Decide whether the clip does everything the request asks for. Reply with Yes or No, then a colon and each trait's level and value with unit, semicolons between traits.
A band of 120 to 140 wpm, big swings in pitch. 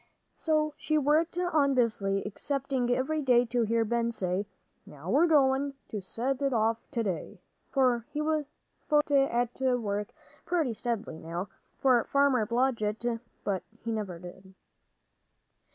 No: slow, 135 wpm; average, 4.7 semitones